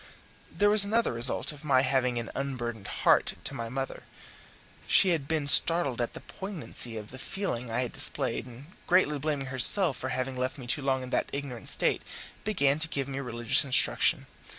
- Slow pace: No, average, 190 wpm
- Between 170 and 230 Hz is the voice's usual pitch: No, low, 135 Hz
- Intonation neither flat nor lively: Yes, average, 3.5 semitones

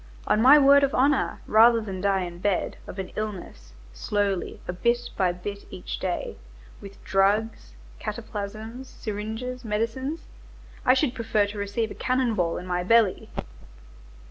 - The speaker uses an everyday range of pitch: Yes, average, 3.8 semitones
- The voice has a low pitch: No, high, 210 Hz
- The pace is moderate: Yes, average, 150 wpm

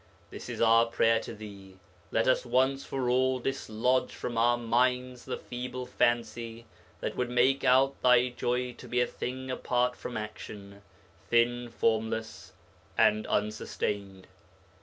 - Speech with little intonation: Yes, narrow, 2.1 semitones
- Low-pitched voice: Yes, low, 120 Hz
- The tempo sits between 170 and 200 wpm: No, average, 140 wpm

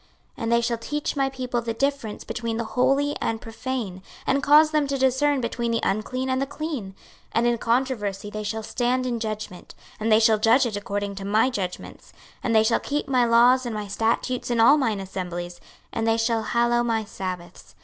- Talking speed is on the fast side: Yes, fast, 210 wpm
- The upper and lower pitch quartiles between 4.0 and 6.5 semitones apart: No, average, 3.3 semitones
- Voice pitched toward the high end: Yes, high, 230 Hz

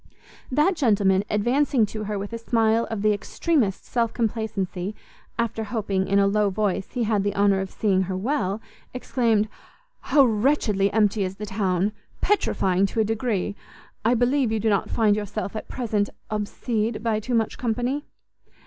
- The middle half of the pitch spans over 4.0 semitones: No, average, 2.7 semitones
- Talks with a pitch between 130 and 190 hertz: No, high, 215 Hz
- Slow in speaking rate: No, average, 165 wpm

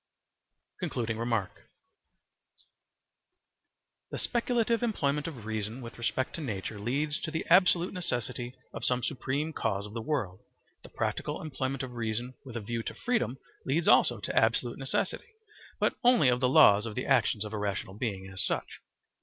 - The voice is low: Yes, low, 125 Hz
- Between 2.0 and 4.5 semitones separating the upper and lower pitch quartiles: No, average, 5.2 semitones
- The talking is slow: No, average, 160 wpm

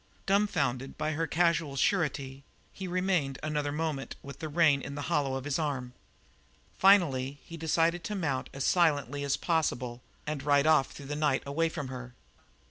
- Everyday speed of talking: Yes, average, 170 wpm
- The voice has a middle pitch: Yes, medium, 150 Hz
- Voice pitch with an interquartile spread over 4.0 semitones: No, average, 3.3 semitones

